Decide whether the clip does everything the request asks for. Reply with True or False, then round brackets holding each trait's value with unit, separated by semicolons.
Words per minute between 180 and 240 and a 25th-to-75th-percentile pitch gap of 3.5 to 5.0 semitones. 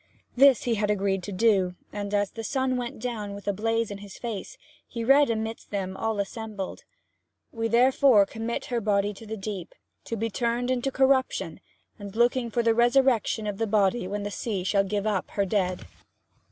False (190 wpm; 2.9 semitones)